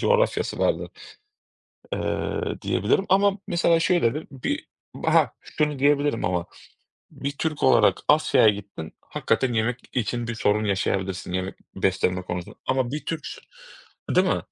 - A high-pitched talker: No, low, 125 Hz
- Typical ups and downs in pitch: No, wide, 7.6 semitones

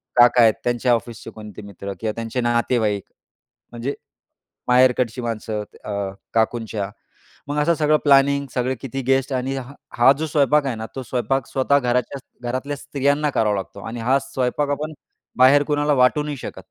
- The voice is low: Yes, low, 125 Hz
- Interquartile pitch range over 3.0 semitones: Yes, average, 3.6 semitones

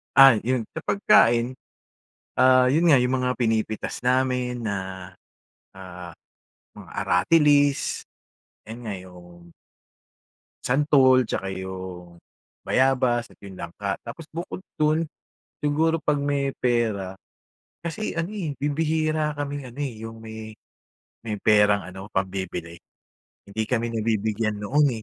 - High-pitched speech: No, low, 120 Hz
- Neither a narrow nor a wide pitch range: No, wide, 6.2 semitones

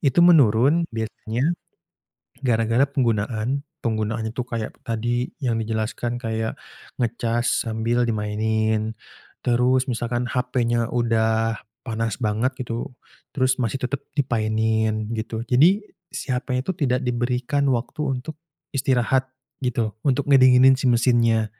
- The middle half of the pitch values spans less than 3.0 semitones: Yes, narrow, 2.5 semitones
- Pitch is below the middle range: Yes, low, 120 Hz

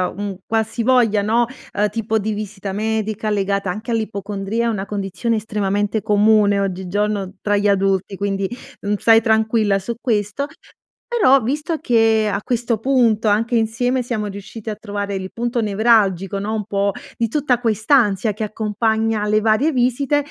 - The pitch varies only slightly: Yes, narrow, 2.3 semitones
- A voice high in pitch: Yes, high, 215 Hz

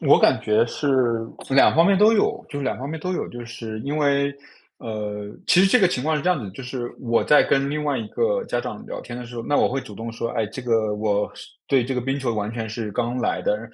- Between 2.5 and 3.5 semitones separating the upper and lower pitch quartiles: No, average, 4.4 semitones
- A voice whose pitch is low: Yes, low, 125 Hz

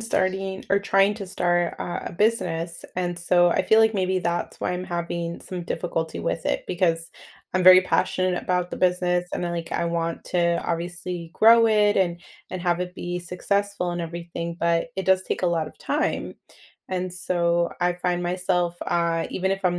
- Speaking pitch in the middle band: Yes, medium, 180 Hz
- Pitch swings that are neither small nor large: No, narrow, 1.4 semitones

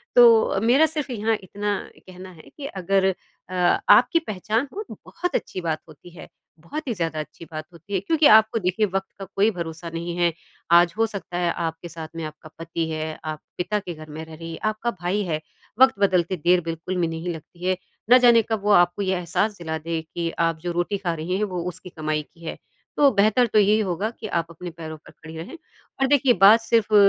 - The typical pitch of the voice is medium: Yes, medium, 180 Hz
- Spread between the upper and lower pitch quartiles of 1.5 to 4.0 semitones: No, average, 4.4 semitones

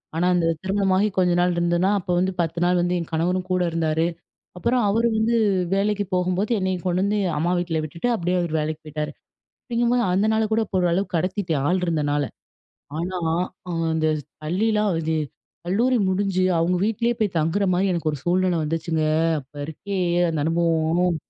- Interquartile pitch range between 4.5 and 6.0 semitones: No, average, 3.2 semitones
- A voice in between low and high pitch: Yes, medium, 180 Hz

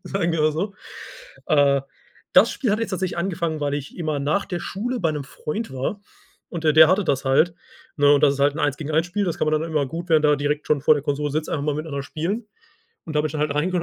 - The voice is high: No, medium, 155 Hz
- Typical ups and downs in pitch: Yes, average, 3.1 semitones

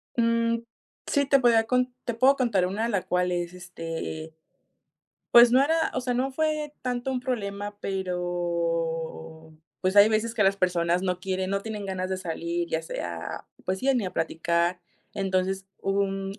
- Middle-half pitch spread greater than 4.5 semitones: Yes, average, 5.0 semitones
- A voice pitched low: No, high, 195 Hz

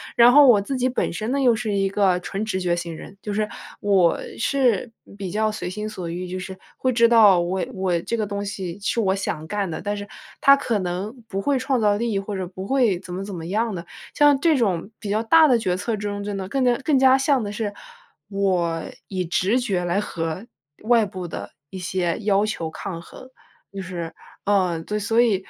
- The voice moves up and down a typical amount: Yes, average, 3.8 semitones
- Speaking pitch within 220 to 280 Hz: No, high, 200 Hz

